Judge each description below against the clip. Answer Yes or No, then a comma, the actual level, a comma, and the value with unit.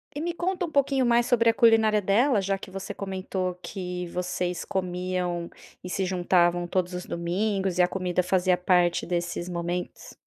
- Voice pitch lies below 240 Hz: Yes, medium, 185 Hz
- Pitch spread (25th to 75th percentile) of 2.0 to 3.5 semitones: Yes, average, 2.9 semitones